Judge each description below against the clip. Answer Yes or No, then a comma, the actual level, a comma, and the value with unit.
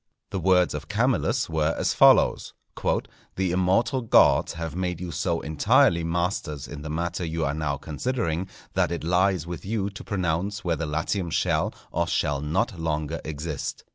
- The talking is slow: No, average, 165 wpm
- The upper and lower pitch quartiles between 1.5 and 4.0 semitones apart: Yes, average, 3.3 semitones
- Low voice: Yes, very low, 85 Hz